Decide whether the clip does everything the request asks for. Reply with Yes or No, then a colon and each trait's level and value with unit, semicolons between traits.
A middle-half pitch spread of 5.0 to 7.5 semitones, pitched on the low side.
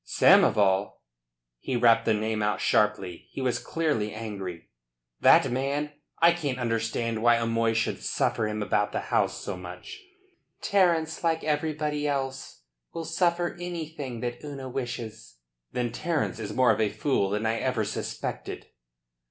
Yes: wide, 5.5 semitones; low, 120 Hz